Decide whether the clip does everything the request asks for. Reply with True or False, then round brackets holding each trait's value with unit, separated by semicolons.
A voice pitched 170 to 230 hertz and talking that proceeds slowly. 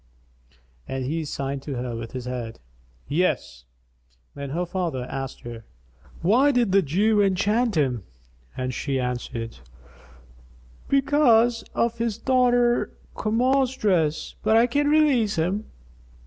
True (185 Hz; 125 wpm)